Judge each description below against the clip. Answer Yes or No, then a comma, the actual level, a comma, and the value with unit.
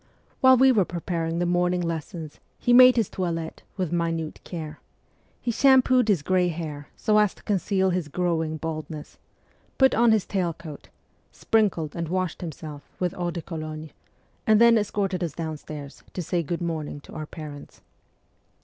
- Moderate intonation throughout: Yes, average, 3.7 semitones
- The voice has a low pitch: No, medium, 175 Hz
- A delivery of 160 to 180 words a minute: Yes, average, 170 wpm